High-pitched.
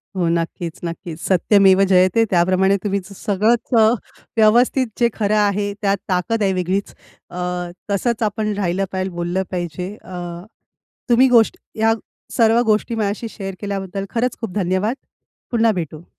Yes: high, 200 Hz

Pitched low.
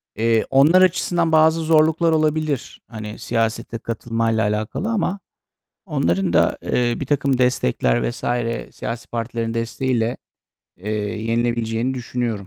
Yes: low, 120 Hz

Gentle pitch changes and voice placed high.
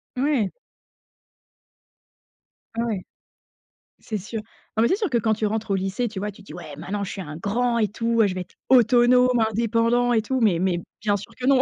No: average, 3.5 semitones; high, 220 Hz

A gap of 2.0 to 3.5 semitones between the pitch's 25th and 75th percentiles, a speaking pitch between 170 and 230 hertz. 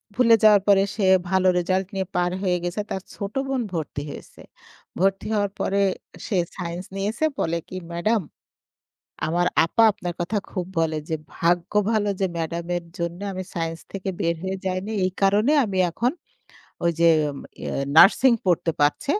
Yes: average, 2.8 semitones; medium, 185 Hz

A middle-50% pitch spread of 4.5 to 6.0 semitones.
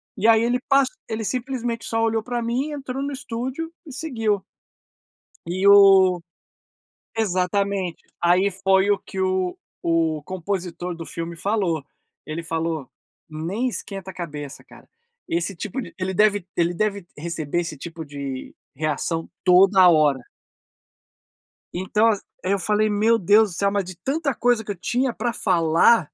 Yes: average, 4.8 semitones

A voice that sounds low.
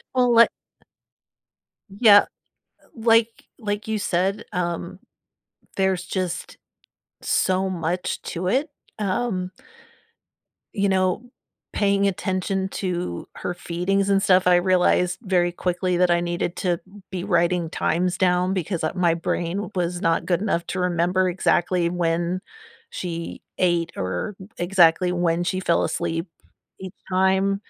No: medium, 180 Hz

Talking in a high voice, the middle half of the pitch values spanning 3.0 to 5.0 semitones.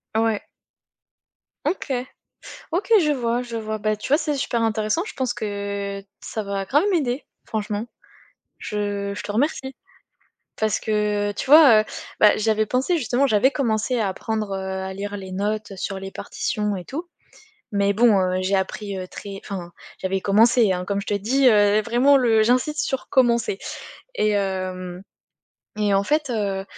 Yes: high, 215 Hz; average, 3.5 semitones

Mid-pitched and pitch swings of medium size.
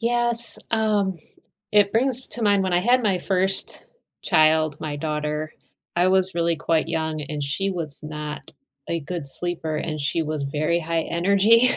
Yes: medium, 170 Hz; average, 4.4 semitones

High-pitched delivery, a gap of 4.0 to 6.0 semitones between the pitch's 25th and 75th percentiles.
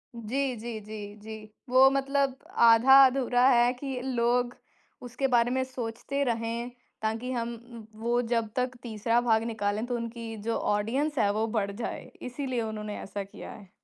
No: high, 235 Hz; narrow, 2.4 semitones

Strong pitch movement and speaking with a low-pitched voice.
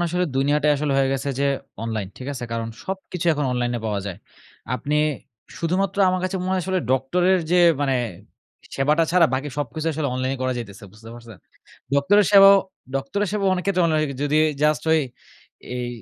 No: wide, 5.9 semitones; medium, 145 Hz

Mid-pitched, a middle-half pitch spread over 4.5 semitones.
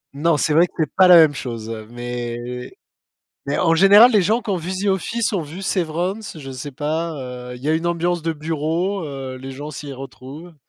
Yes: medium, 155 Hz; average, 4.9 semitones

